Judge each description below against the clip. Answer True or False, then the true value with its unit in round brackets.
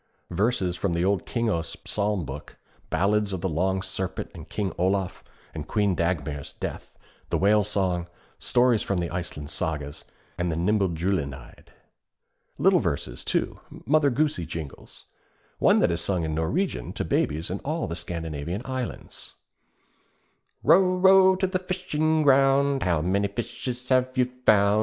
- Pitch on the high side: False (100 Hz)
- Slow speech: False (145 wpm)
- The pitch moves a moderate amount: False (7.0 semitones)